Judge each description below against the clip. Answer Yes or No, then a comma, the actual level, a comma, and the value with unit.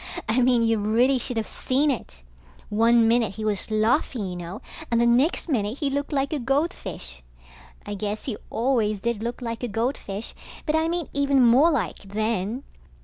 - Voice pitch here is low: No, high, 235 Hz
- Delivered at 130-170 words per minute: No, average, 185 wpm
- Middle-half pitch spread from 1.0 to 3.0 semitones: No, average, 4.1 semitones